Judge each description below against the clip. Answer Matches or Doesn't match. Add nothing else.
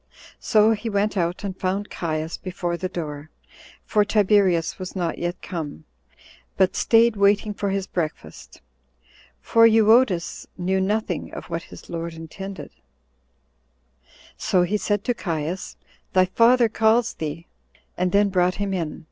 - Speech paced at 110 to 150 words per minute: Matches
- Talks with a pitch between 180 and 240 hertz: Matches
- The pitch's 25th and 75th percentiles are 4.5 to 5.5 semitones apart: Doesn't match